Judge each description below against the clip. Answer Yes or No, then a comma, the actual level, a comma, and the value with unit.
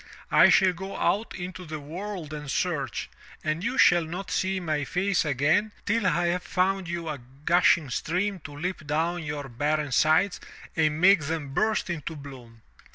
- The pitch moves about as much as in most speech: Yes, average, 3.8 semitones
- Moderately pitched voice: Yes, medium, 165 Hz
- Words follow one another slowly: No, average, 170 wpm